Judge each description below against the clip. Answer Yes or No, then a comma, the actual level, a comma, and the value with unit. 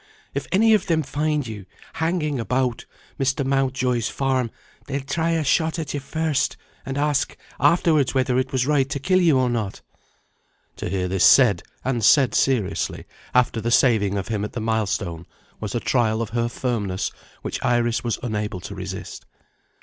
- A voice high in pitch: No, low, 125 Hz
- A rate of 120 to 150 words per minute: No, average, 175 wpm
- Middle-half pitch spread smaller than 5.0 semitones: Yes, average, 4.4 semitones